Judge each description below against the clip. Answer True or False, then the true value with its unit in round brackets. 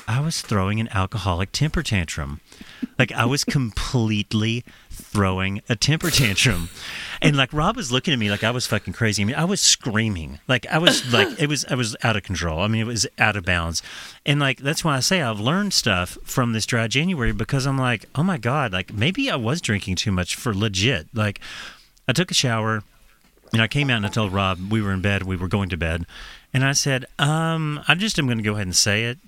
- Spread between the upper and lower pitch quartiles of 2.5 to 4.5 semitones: False (5.5 semitones)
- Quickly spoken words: True (235 wpm)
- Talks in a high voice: False (115 Hz)